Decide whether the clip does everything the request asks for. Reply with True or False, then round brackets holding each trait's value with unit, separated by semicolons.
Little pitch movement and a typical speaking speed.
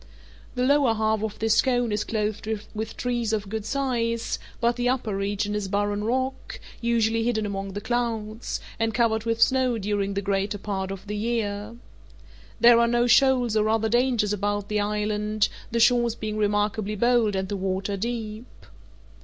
True (2.3 semitones; 170 wpm)